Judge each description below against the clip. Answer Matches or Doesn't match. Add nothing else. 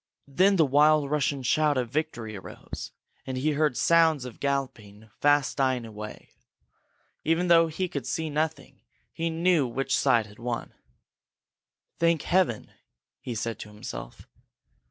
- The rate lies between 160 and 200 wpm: Doesn't match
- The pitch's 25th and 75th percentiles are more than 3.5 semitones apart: Matches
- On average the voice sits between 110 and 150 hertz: Matches